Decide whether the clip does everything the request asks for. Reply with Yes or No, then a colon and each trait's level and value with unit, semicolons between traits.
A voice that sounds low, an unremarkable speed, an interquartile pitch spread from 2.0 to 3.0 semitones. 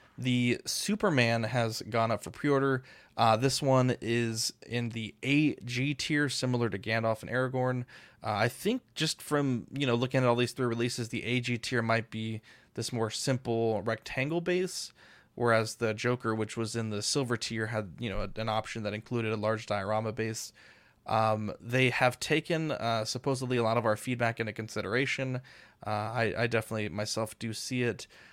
Yes: low, 115 Hz; average, 180 wpm; narrow, 2.5 semitones